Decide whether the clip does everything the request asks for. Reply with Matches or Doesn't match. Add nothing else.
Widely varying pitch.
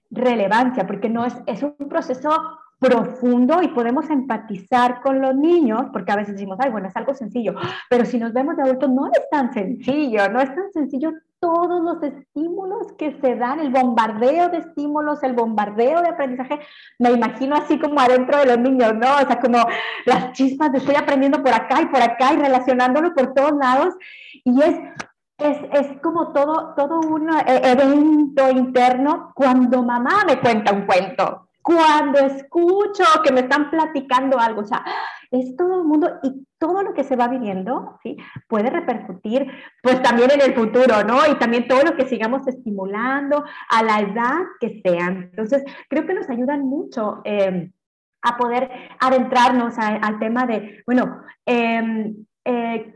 Doesn't match